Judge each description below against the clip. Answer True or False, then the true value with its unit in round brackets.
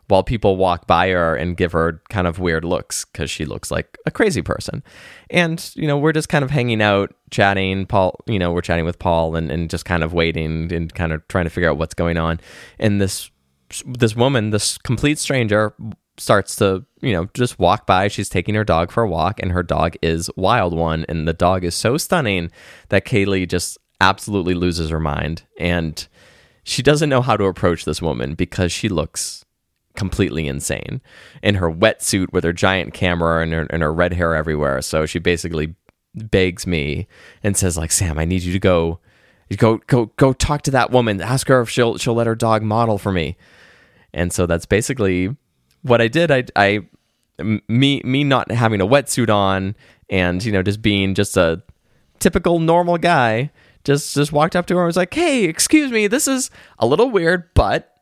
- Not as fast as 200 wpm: False (205 wpm)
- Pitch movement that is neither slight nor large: False (5.9 semitones)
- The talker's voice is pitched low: True (95 Hz)